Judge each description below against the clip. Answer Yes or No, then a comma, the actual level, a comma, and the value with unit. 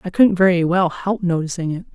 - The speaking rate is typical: No, fast, 215 wpm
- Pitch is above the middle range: No, medium, 180 Hz